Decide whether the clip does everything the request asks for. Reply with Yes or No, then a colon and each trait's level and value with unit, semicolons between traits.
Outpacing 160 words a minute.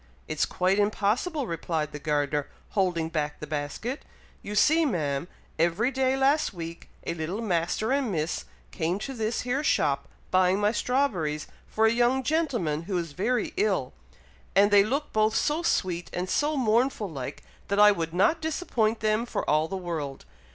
Yes: average, 170 wpm